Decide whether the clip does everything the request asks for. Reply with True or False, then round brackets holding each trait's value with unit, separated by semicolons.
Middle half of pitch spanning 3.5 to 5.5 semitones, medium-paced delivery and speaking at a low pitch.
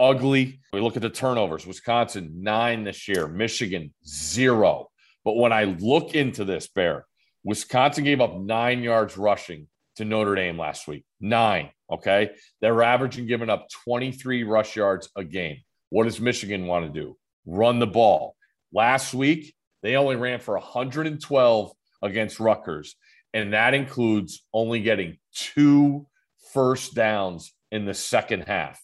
True (4.0 semitones; 150 wpm; 115 Hz)